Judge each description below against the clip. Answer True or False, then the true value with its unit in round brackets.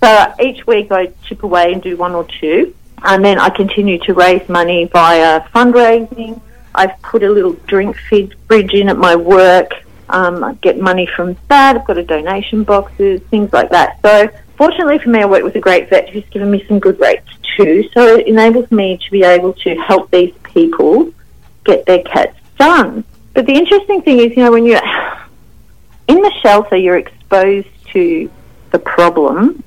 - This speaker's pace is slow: False (190 wpm)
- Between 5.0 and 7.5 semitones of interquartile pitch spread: True (5.3 semitones)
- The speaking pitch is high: True (205 Hz)